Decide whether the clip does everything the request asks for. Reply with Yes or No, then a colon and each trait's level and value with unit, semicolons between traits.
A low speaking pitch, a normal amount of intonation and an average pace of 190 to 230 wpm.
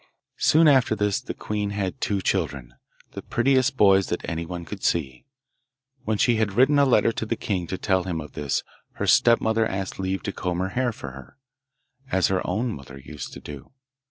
Yes: very low, 95 Hz; average, 4.7 semitones; average, 195 wpm